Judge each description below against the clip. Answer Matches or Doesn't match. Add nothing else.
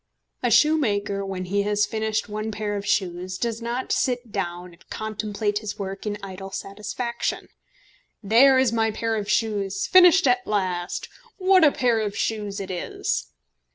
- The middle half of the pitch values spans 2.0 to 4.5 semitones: Matches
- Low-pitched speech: Doesn't match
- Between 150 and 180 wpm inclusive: Matches